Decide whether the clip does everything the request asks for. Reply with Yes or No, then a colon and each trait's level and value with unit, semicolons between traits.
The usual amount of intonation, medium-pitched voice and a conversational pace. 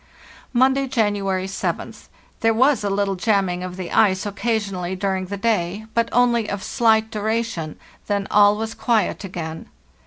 No: average, 3.0 semitones; high, 205 Hz; average, 150 wpm